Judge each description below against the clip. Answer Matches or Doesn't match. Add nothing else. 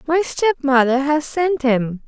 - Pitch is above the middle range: Matches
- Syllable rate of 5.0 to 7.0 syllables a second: Doesn't match